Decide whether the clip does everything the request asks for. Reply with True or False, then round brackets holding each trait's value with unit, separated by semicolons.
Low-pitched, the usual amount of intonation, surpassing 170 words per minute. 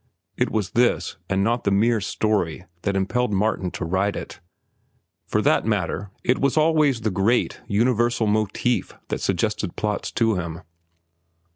False (105 Hz; 3.6 semitones; 150 wpm)